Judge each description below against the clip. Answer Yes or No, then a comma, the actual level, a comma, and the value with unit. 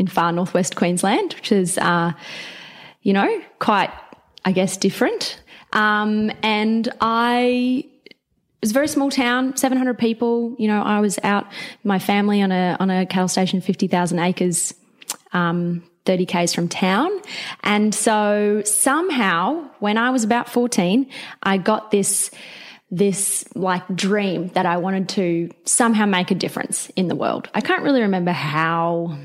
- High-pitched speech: Yes, high, 205 Hz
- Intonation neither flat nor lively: Yes, average, 4.6 semitones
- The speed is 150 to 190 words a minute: Yes, average, 160 wpm